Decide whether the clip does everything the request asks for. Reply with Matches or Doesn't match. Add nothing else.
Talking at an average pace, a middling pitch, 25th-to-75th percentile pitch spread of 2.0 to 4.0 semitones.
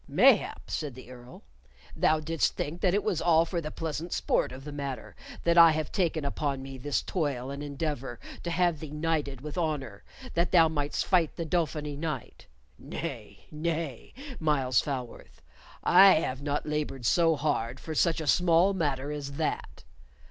Matches